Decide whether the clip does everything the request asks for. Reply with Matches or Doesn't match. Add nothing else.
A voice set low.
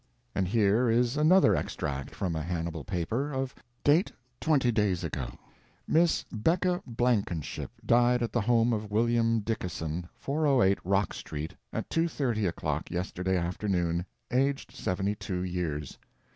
Matches